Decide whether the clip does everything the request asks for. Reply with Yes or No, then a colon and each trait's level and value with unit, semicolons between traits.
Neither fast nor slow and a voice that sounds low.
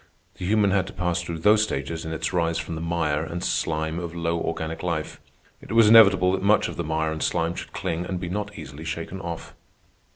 No: fast, 225 wpm; very low, 85 Hz